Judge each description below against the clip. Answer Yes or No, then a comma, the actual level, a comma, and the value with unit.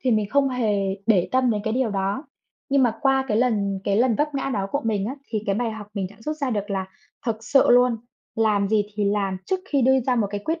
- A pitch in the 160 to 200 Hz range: No, high, 225 Hz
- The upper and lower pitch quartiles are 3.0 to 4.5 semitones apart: Yes, average, 4.2 semitones